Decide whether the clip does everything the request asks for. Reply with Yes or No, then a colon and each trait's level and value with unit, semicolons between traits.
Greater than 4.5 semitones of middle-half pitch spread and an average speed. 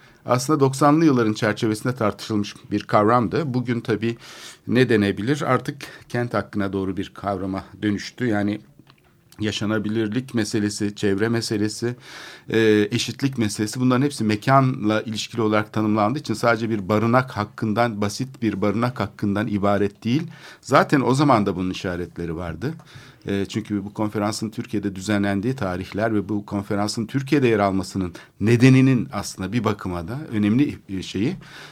No: average, 3.0 semitones; average, 130 wpm